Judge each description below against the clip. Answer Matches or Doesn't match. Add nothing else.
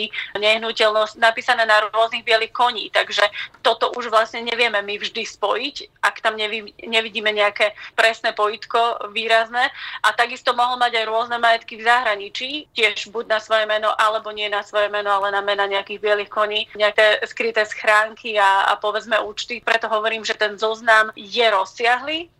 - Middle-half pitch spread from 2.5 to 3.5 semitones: Doesn't match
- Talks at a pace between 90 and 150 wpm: Doesn't match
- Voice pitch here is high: Matches